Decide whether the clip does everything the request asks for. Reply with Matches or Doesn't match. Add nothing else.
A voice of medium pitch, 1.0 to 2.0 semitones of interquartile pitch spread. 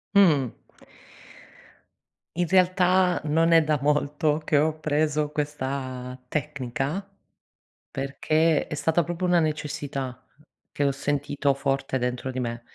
Doesn't match